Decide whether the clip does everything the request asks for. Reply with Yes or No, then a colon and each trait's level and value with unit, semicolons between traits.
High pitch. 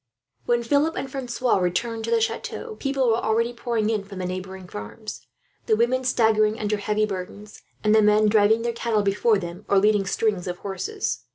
Yes: high, 215 Hz